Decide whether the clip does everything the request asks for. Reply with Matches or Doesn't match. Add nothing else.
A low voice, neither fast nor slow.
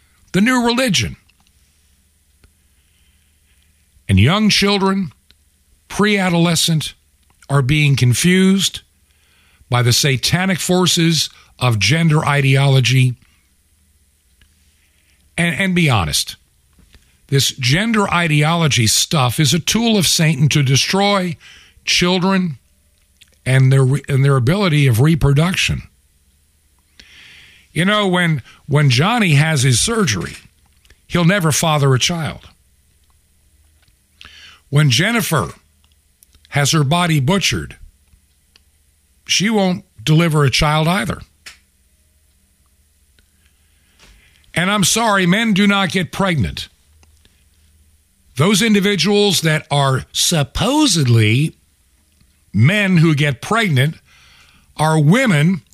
Doesn't match